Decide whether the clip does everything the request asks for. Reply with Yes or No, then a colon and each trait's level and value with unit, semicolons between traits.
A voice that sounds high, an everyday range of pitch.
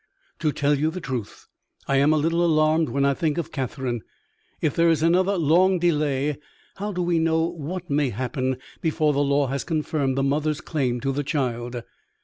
No: medium, 150 Hz; average, 3.3 semitones